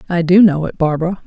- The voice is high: No, medium, 170 Hz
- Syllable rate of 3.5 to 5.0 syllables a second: No, 6.5 syllables/s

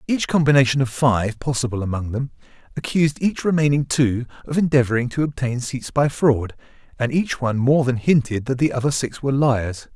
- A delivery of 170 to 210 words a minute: Yes, average, 180 wpm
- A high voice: No, low, 130 Hz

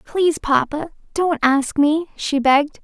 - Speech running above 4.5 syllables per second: No, 4.3 syllables/s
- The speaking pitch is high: Yes, very high, 300 Hz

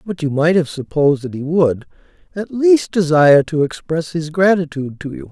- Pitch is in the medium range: Yes, medium, 160 Hz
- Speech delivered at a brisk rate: No, average, 190 wpm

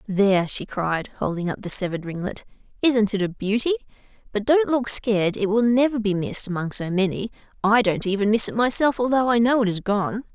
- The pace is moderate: No, fast, 210 wpm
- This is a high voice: Yes, high, 215 Hz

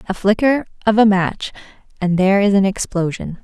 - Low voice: No, high, 200 Hz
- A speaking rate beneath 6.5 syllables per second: Yes, 5.5 syllables/s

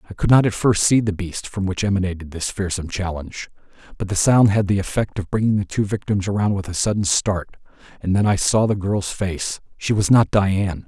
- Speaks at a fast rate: Yes, fast, 220 wpm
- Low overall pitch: Yes, low, 100 Hz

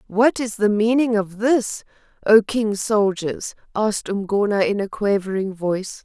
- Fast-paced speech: No, average, 150 wpm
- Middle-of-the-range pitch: No, high, 210 Hz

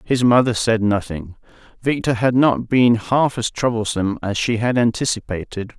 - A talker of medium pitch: No, low, 115 Hz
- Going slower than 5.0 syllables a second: Yes, 4.8 syllables/s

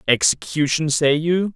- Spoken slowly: Yes, slow, 115 wpm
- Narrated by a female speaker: No, male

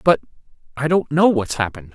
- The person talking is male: Yes, male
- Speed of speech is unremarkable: Yes, average, 185 wpm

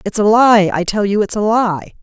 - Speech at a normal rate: No, fast, 235 wpm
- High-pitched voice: Yes, high, 205 Hz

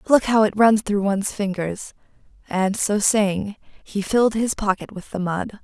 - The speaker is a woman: Yes, female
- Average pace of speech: Yes, average, 180 wpm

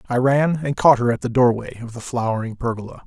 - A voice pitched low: Yes, low, 125 Hz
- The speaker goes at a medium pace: No, fast, 235 wpm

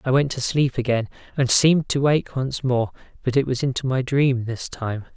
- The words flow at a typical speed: No, fast, 220 wpm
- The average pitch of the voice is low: Yes, low, 130 Hz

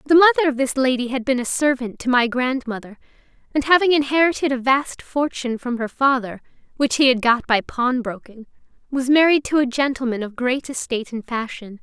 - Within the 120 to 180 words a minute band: No, average, 195 wpm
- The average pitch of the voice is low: No, very high, 260 Hz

